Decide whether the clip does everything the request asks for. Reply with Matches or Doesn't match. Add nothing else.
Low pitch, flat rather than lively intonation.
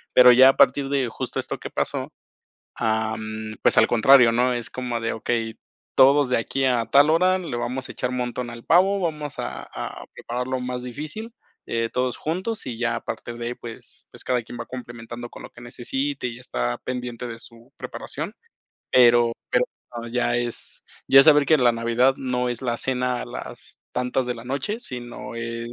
Matches